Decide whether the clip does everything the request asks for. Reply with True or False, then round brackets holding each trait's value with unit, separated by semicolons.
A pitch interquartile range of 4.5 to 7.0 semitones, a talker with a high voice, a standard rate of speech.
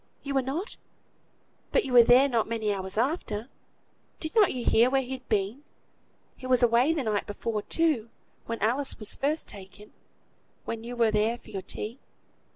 False (3.9 semitones; 240 Hz; 175 wpm)